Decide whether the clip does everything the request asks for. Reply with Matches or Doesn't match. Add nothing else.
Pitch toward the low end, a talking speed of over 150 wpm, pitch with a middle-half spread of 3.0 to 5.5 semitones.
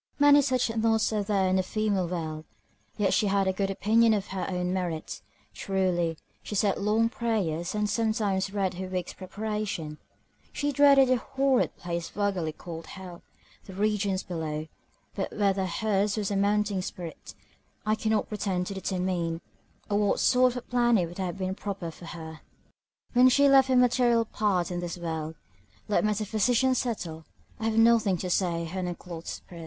Doesn't match